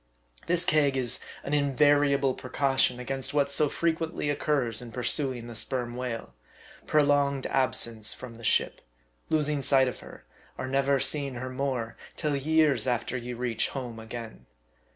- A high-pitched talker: No, low, 135 Hz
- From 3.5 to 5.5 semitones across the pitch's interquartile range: No, average, 2.9 semitones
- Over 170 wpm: No, average, 155 wpm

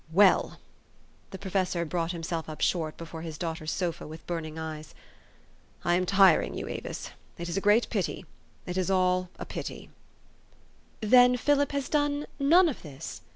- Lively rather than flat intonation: No, average, 4.1 semitones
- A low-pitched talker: No, medium, 180 Hz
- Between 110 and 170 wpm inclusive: Yes, average, 165 wpm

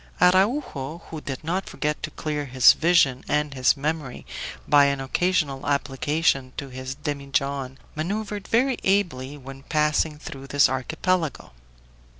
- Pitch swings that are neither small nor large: Yes, average, 3.5 semitones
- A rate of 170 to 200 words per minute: No, slow, 135 wpm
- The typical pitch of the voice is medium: Yes, medium, 145 Hz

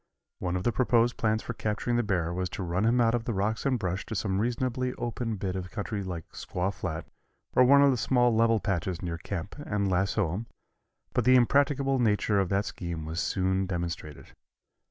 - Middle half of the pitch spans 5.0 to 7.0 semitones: No, average, 4.6 semitones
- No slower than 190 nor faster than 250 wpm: Yes, fast, 205 wpm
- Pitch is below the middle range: Yes, low, 105 Hz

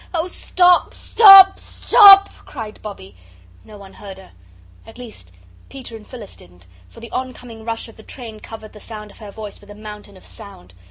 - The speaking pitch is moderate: No, high, 220 Hz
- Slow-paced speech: No, average, 185 wpm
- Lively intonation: No, average, 3.5 semitones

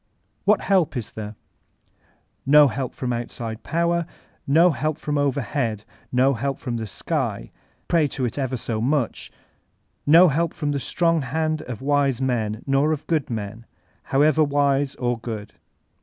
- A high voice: No, low, 135 Hz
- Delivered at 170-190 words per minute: No, average, 155 wpm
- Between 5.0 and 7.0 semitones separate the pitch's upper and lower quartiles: No, average, 4.3 semitones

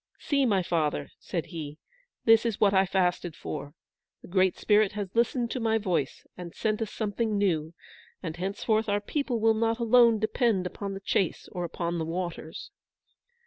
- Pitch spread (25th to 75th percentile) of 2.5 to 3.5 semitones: No, average, 4.2 semitones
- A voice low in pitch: No, high, 200 Hz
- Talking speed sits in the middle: Yes, average, 175 wpm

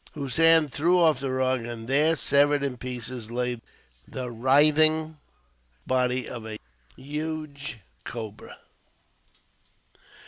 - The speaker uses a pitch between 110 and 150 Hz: Yes, low, 135 Hz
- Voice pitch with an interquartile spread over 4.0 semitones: No, average, 3.7 semitones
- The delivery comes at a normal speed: No, slow, 105 wpm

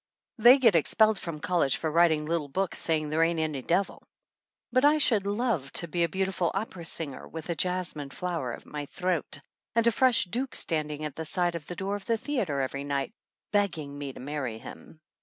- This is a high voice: No, medium, 170 Hz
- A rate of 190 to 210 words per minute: Yes, average, 195 wpm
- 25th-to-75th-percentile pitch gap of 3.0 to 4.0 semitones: No, average, 5.0 semitones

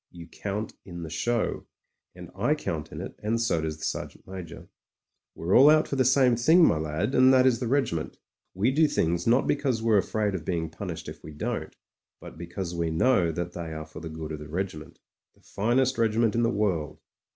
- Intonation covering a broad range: Yes, wide, 6.6 semitones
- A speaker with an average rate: No, fast, 220 wpm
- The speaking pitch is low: Yes, low, 100 Hz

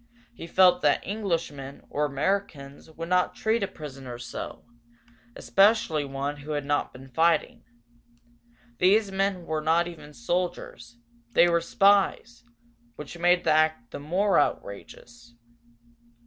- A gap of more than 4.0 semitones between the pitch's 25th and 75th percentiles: Yes, average, 4.7 semitones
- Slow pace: Yes, slow, 130 wpm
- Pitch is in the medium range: Yes, medium, 160 Hz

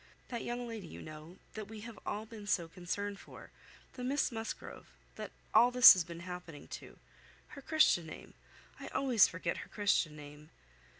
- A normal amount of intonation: No, wide, 5.7 semitones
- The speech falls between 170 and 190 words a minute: Yes, average, 175 wpm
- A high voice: Yes, high, 205 Hz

